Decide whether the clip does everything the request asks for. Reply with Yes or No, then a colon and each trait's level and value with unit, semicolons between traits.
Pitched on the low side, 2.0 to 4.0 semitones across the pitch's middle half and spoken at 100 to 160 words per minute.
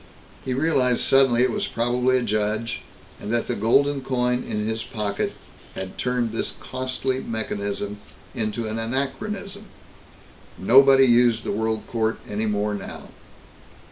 Yes: low, 120 Hz; average, 3.0 semitones; average, 140 wpm